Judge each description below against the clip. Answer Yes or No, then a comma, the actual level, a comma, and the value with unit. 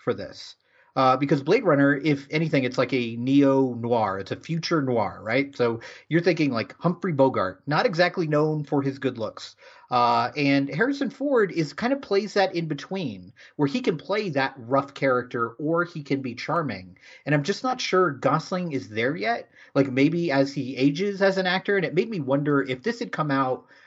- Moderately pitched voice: Yes, medium, 145 Hz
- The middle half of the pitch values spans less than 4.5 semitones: No, average, 5.2 semitones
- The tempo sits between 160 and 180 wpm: No, fast, 205 wpm